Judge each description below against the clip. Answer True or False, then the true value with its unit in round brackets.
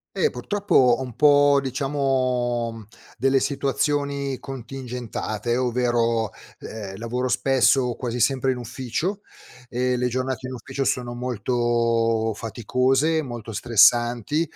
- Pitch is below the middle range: True (125 Hz)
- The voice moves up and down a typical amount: False (2.3 semitones)